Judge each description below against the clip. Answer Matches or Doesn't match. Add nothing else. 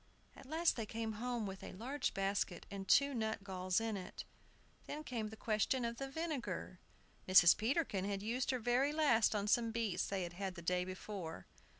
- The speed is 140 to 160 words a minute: Doesn't match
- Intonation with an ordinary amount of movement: Matches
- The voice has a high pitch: Matches